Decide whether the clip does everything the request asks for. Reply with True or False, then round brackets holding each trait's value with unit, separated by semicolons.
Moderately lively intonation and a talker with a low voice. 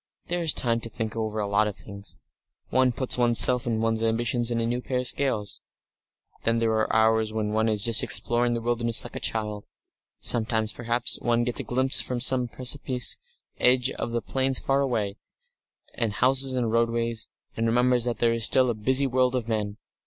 False (2.2 semitones; 115 Hz)